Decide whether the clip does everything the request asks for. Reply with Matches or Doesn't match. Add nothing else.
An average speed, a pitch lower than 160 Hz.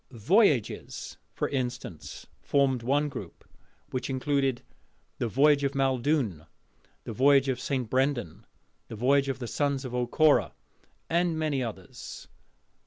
Doesn't match